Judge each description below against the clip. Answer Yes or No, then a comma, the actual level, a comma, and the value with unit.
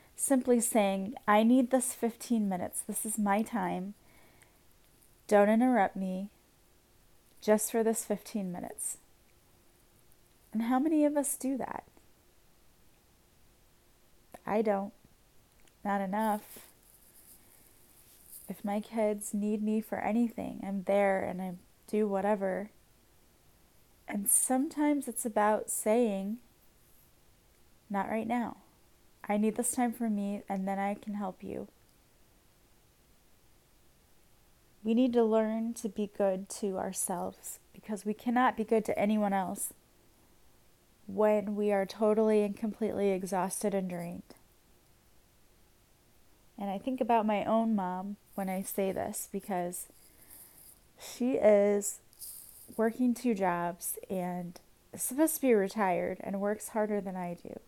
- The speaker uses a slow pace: Yes, slow, 125 wpm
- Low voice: No, high, 210 Hz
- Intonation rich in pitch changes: No, narrow, 2.6 semitones